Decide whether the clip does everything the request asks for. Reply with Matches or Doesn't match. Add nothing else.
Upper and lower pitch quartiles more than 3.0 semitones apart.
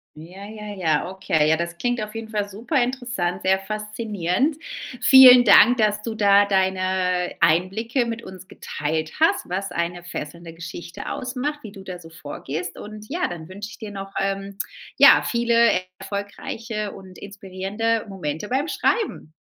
Matches